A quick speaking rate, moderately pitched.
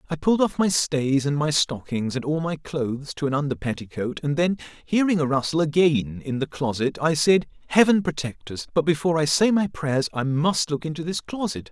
Yes: fast, 215 wpm; medium, 150 Hz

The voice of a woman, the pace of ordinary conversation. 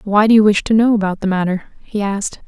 No: female; fast, 265 wpm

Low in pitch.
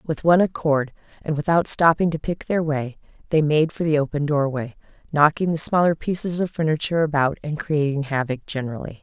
No: medium, 150 Hz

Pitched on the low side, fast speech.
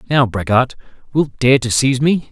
No: low, 130 Hz; average, 180 wpm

